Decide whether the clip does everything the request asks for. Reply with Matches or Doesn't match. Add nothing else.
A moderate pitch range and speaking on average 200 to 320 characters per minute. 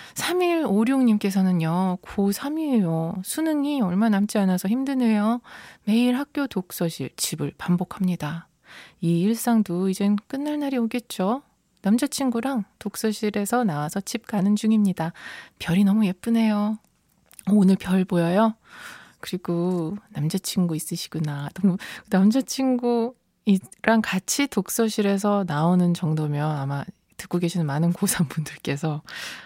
Matches